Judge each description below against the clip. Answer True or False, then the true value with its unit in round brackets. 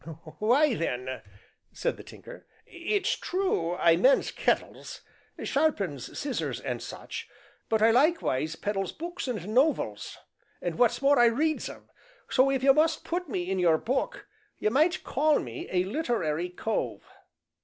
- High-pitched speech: True (240 Hz)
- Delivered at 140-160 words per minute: True (150 wpm)